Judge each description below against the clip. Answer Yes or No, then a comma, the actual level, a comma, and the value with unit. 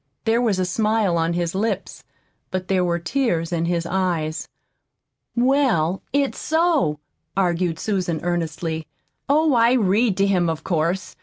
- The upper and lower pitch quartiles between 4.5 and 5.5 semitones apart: Yes, average, 5.0 semitones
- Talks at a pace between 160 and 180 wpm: No, average, 145 wpm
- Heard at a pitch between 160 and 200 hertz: Yes, medium, 185 Hz